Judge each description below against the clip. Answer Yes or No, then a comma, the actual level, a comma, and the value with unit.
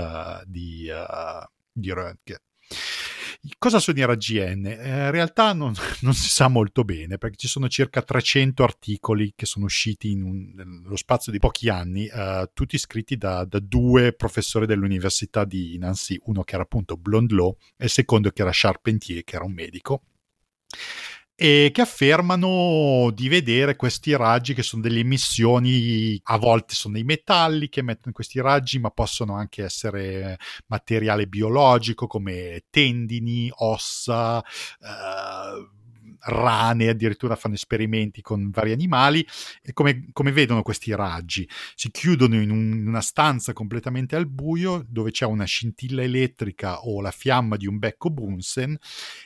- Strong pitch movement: No, average, 4.4 semitones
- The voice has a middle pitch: No, low, 115 Hz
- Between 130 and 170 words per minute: Yes, average, 150 wpm